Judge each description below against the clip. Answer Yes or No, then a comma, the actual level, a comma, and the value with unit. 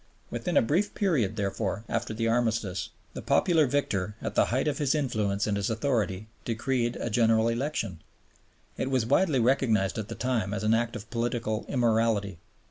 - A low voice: Yes, low, 115 Hz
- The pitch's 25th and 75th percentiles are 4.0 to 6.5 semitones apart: No, average, 3.3 semitones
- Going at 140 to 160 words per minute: No, average, 175 wpm